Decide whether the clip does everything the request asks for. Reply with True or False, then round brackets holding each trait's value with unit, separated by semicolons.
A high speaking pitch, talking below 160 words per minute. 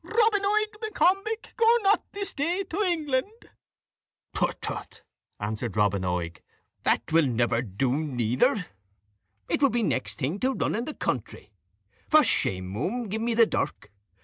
True (230 Hz; 150 wpm)